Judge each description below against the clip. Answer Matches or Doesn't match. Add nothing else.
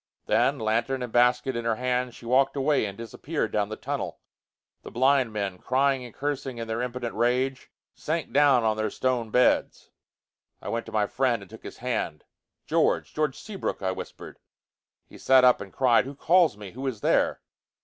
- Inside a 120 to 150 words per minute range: Doesn't match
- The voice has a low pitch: Matches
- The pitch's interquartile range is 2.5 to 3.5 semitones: Matches